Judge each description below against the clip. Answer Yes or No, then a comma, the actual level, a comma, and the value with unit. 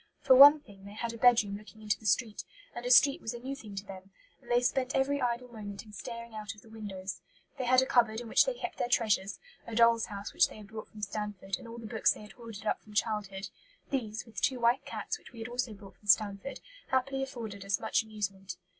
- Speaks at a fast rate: Yes, fast, 250 wpm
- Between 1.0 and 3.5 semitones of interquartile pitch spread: Yes, average, 3.0 semitones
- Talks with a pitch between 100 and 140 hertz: No, high, 220 Hz